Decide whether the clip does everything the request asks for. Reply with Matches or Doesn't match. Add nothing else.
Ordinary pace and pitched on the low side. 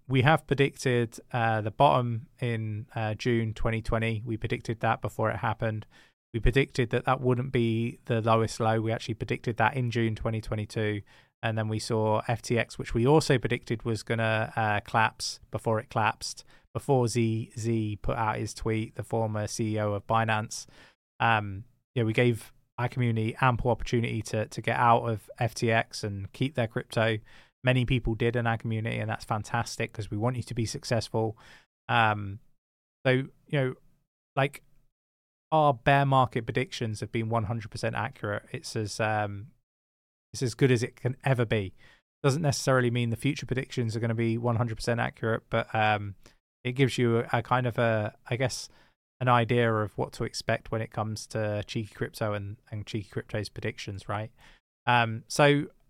Matches